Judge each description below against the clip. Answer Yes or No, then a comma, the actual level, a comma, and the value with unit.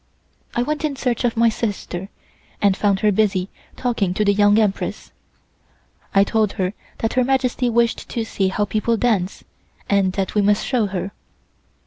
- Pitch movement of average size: Yes, average, 3.1 semitones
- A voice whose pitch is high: Yes, high, 210 Hz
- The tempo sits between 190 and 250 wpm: No, average, 170 wpm